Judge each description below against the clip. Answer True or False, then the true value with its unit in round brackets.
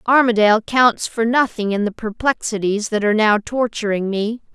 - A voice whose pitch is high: True (220 Hz)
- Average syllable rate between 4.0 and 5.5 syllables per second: True (5.1 syllables/s)